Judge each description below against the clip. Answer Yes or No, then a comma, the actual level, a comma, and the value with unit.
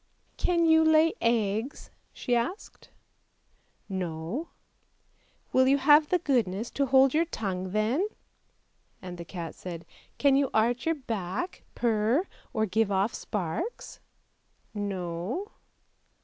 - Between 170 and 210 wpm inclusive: No, average, 150 wpm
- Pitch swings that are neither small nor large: No, wide, 7.2 semitones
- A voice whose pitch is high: Yes, high, 235 Hz